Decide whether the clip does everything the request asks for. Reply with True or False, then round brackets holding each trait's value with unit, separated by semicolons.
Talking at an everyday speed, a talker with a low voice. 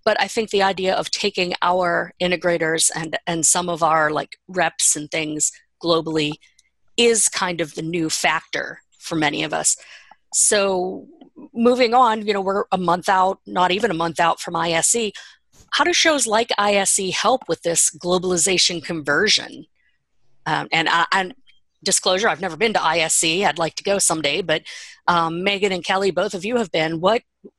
False (175 wpm; 180 Hz)